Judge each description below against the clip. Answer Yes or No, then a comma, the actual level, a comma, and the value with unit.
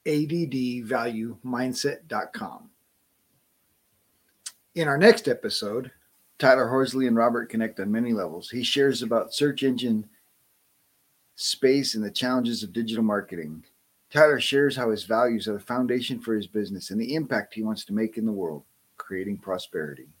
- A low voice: Yes, low, 120 Hz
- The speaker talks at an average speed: Yes, average, 145 wpm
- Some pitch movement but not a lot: Yes, average, 3.3 semitones